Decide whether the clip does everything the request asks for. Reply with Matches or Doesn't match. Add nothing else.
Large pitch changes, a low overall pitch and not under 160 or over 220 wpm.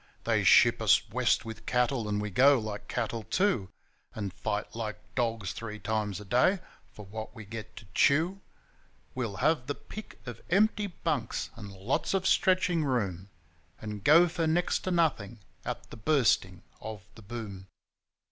Matches